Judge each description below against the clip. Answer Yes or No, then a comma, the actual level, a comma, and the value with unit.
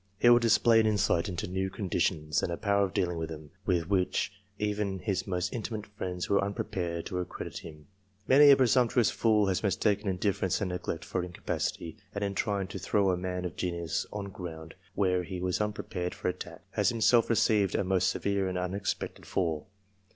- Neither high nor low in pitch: No, very low, 95 Hz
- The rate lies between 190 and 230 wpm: Yes, average, 195 wpm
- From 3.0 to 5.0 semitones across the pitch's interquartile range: No, narrow, 2.6 semitones